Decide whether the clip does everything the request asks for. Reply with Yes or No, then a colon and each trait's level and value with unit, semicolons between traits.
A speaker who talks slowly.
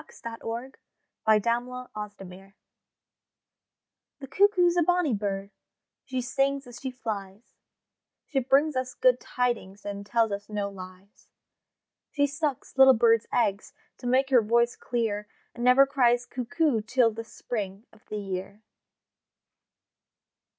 Yes: slow, 130 wpm